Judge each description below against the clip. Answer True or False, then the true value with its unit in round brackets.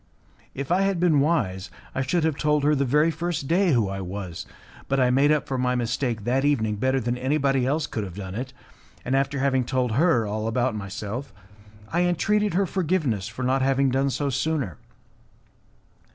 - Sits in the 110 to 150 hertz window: True (135 Hz)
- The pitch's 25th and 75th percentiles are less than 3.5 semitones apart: False (4.6 semitones)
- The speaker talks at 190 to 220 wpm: True (195 wpm)